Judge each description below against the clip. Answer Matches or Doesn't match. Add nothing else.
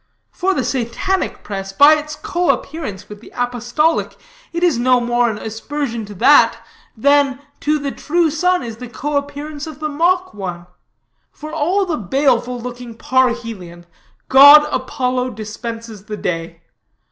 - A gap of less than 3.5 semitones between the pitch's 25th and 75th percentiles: Doesn't match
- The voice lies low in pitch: Doesn't match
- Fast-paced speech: Doesn't match